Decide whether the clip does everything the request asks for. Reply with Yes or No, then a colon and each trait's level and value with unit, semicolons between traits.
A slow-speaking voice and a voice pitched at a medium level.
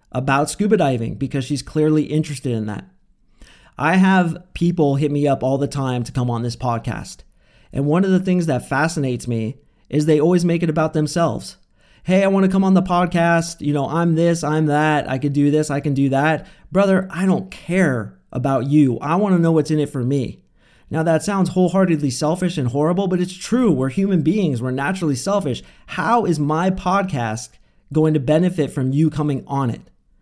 No: average, 200 wpm; medium, 155 Hz